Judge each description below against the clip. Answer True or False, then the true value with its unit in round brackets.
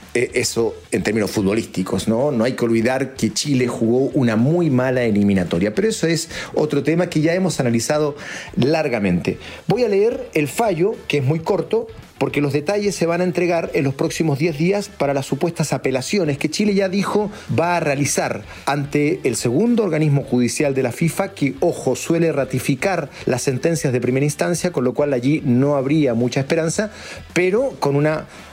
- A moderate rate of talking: True (180 wpm)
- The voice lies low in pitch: False (145 Hz)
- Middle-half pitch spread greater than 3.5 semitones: True (5.0 semitones)